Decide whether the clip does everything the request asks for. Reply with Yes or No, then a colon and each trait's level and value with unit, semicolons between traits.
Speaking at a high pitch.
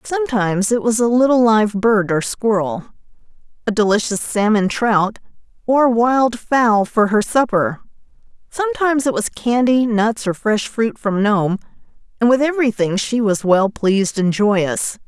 Yes: high, 220 Hz